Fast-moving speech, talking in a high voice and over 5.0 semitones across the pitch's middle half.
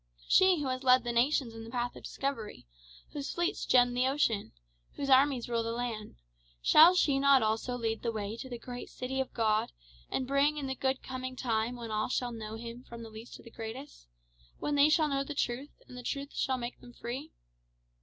No: fast, 215 wpm; very high, 250 Hz; average, 3.0 semitones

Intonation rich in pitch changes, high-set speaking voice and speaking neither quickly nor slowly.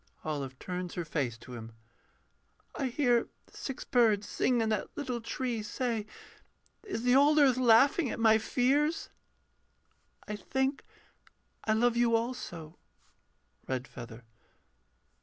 No: wide, 6.3 semitones; high, 230 Hz; slow, 120 wpm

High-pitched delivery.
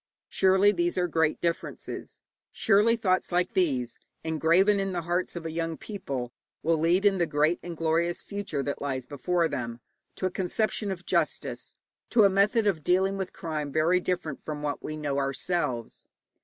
No: medium, 170 Hz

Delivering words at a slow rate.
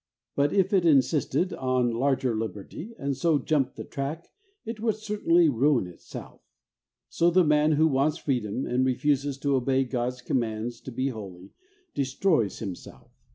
No: average, 155 wpm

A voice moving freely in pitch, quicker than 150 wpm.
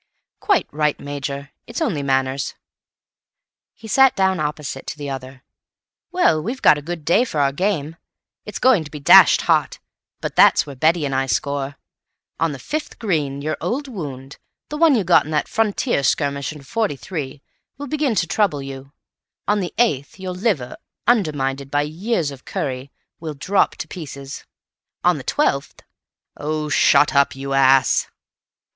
Yes: wide, 5.9 semitones; average, 165 wpm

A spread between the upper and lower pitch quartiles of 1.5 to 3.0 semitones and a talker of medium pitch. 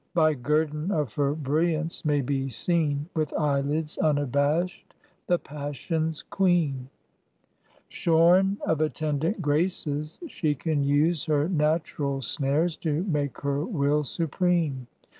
Yes: narrow, 2.5 semitones; medium, 150 Hz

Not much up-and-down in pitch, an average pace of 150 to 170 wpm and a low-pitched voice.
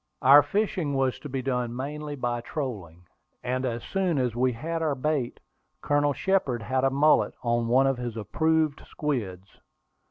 No: average, 3.7 semitones; average, 165 wpm; low, 130 Hz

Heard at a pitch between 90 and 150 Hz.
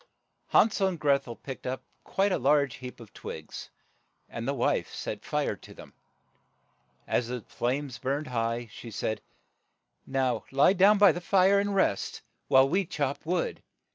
Yes: medium, 140 Hz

